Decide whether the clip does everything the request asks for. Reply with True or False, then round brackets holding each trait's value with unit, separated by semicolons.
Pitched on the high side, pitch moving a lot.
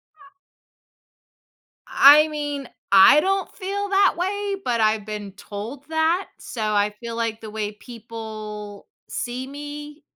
True (250 Hz; 6.8 semitones)